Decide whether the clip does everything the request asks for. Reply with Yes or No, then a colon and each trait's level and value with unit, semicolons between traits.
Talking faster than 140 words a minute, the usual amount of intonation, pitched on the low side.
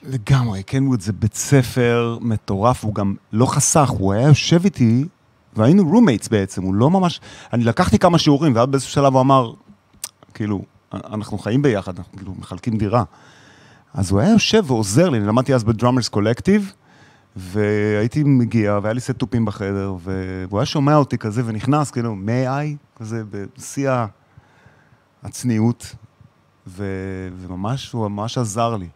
Yes: fast, 150 wpm; average, 4.6 semitones; low, 115 Hz